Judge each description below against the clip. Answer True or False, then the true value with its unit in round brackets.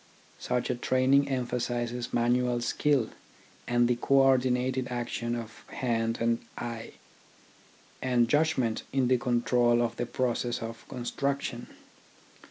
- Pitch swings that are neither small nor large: False (1.4 semitones)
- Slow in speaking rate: True (125 wpm)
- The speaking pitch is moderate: False (120 Hz)